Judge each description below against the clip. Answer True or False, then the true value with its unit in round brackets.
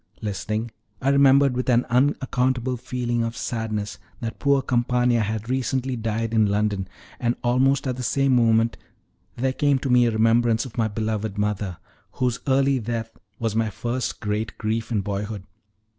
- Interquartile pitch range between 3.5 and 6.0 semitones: False (2.7 semitones)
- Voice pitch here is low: True (120 Hz)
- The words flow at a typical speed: True (160 wpm)